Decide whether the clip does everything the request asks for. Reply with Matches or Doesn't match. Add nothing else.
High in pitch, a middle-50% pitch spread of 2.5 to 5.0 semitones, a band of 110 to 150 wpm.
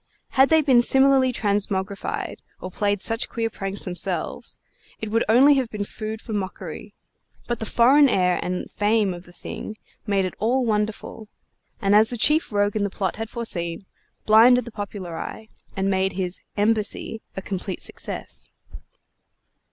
Doesn't match